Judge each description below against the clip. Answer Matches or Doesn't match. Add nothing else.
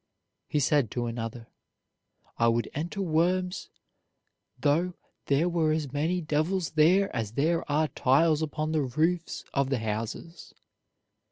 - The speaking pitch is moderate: Matches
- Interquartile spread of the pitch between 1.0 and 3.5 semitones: Doesn't match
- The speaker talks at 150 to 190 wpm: Doesn't match